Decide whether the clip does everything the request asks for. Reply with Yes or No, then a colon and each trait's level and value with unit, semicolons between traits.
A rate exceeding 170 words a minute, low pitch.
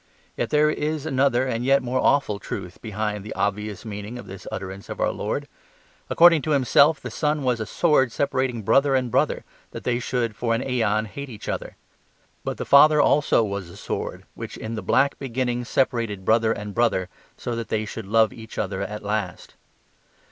Yes: average, 190 wpm; low, 115 Hz